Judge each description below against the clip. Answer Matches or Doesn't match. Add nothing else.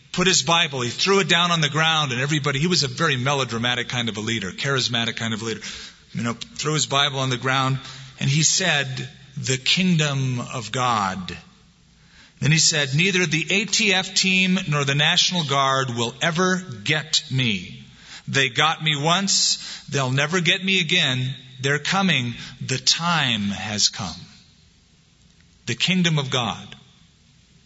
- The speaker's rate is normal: Matches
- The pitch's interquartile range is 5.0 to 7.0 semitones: Matches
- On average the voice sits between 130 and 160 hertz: Matches